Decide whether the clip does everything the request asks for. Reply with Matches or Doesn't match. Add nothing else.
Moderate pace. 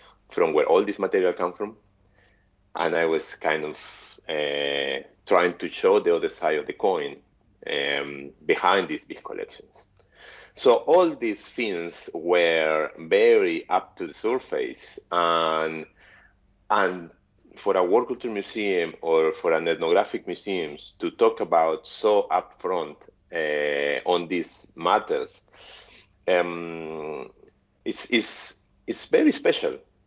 Doesn't match